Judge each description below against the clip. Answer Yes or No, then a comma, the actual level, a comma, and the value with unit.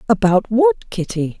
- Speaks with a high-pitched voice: Yes, high, 225 Hz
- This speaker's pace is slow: Yes, slow, 130 wpm